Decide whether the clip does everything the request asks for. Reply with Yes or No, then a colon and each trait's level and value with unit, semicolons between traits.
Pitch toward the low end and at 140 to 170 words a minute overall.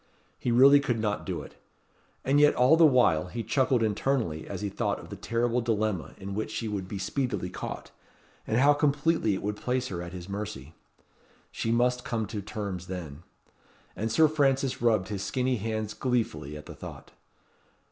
No: low, 110 Hz; average, 185 wpm